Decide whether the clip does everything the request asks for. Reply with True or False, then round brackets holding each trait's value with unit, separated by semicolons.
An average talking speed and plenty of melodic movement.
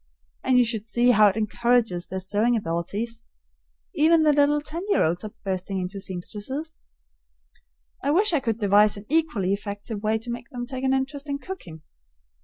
True (180 wpm; 5.7 semitones)